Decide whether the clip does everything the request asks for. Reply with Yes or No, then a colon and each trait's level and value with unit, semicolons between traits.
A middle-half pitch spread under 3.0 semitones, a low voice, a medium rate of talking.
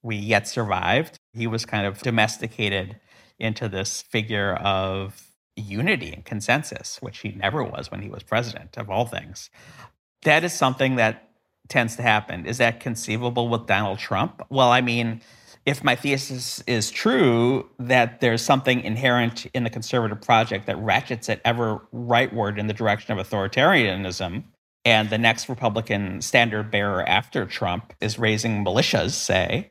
Yes: narrow, 2.5 semitones; low, 115 Hz; average, 155 wpm